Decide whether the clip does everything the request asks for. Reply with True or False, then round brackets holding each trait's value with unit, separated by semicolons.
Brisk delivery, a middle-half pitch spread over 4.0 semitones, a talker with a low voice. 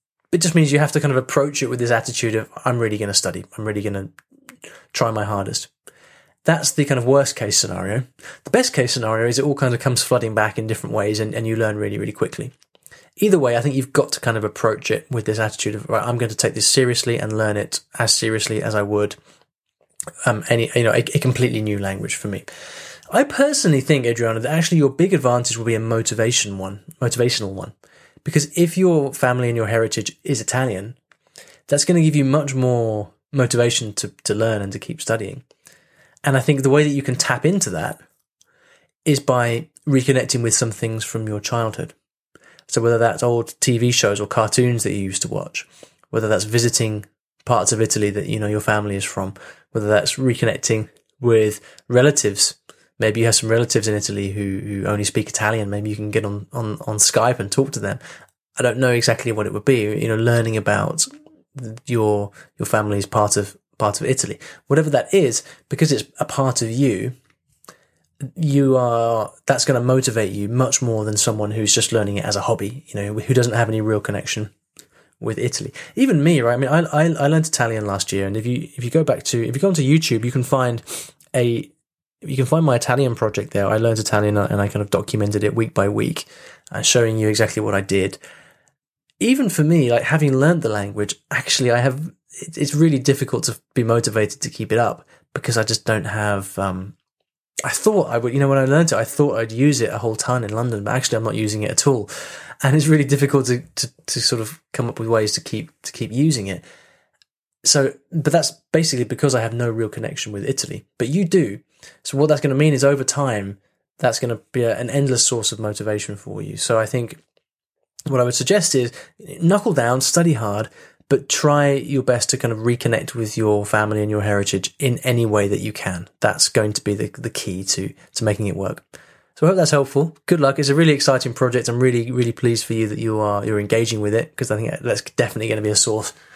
True (225 wpm; 4.6 semitones; 120 Hz)